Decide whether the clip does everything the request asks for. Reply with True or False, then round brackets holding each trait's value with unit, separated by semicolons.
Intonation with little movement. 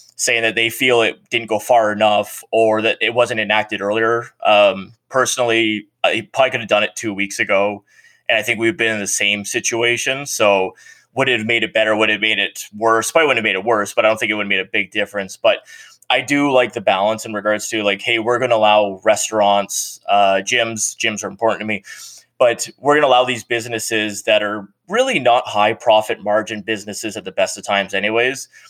True (2.1 semitones)